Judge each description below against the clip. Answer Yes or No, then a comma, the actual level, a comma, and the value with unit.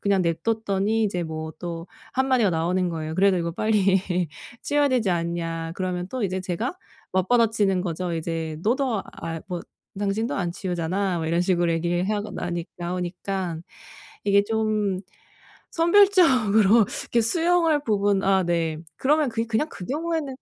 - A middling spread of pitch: Yes, average, 4.5 semitones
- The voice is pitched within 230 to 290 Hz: No, high, 195 Hz